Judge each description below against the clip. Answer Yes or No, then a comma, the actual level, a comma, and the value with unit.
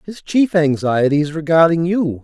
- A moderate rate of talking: Yes, average, 160 wpm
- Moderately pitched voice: Yes, medium, 165 Hz